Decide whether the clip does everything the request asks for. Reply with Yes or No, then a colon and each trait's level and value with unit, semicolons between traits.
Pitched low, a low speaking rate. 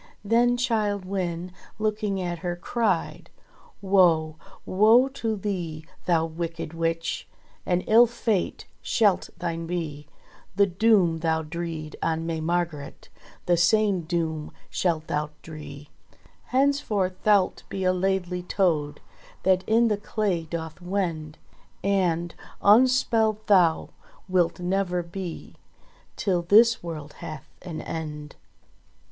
No: medium, 180 Hz; slow, 115 wpm